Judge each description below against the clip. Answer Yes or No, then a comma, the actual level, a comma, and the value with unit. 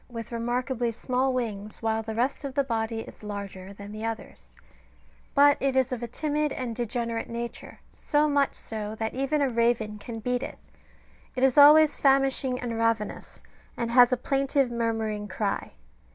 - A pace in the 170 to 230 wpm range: Yes, average, 175 wpm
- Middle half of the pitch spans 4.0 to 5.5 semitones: No, average, 3.1 semitones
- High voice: Yes, high, 235 Hz